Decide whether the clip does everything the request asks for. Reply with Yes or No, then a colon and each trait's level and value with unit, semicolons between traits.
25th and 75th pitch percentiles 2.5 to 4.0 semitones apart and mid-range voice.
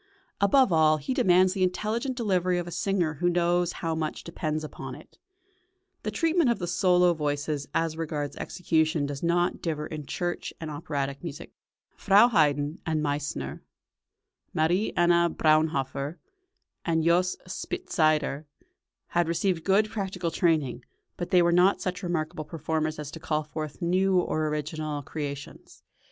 Yes: average, 3.1 semitones; medium, 165 Hz